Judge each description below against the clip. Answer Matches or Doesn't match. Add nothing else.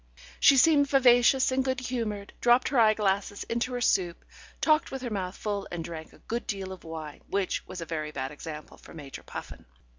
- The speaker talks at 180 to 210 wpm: Matches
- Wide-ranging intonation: Matches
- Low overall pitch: Doesn't match